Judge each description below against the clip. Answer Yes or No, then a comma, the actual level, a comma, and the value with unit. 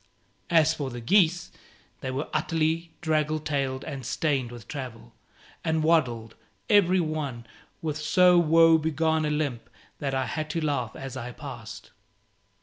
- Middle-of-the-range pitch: Yes, medium, 150 Hz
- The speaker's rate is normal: Yes, average, 145 wpm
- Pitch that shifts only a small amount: No, average, 3.6 semitones